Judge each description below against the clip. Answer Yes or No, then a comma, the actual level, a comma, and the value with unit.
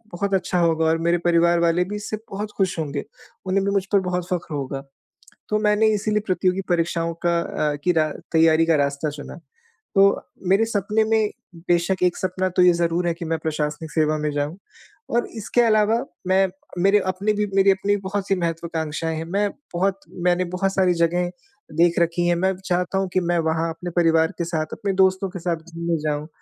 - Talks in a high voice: No, medium, 175 Hz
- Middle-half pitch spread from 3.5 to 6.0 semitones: No, average, 2.9 semitones